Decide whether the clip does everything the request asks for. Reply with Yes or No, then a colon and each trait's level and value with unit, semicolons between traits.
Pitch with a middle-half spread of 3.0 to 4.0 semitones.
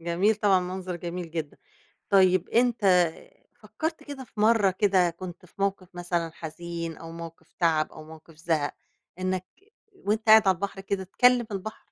Yes: average, 3.3 semitones